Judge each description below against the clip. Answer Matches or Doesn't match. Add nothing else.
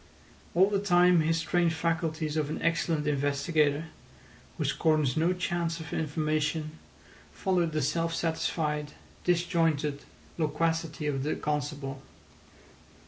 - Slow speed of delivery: Matches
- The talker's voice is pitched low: Doesn't match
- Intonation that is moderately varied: Doesn't match